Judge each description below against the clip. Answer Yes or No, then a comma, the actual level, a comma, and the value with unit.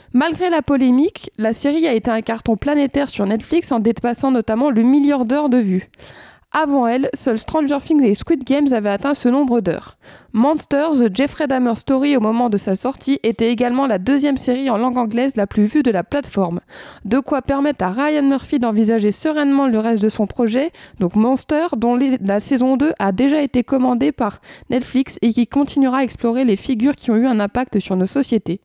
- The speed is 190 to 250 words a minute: Yes, average, 205 wpm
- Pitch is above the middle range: Yes, very high, 255 Hz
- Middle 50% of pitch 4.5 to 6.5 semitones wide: No, average, 3.8 semitones